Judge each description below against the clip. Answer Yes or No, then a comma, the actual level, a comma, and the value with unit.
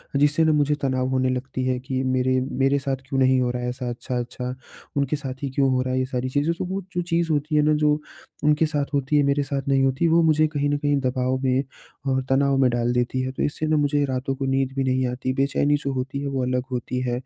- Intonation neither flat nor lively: No, narrow, 2.1 semitones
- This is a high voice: No, low, 135 Hz